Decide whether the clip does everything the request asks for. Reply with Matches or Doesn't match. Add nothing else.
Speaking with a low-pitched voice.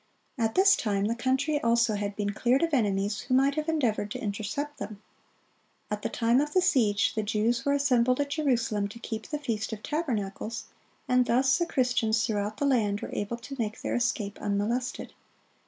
Doesn't match